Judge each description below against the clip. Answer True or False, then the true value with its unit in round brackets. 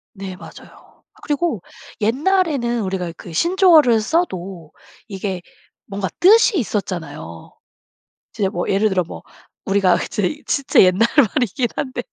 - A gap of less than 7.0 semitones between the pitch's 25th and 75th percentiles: False (7.4 semitones)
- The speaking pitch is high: True (210 Hz)